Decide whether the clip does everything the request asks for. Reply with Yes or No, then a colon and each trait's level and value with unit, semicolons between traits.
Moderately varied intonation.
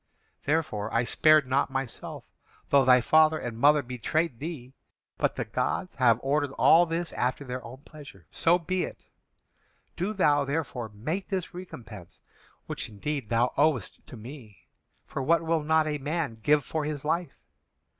Yes: average, 4.3 semitones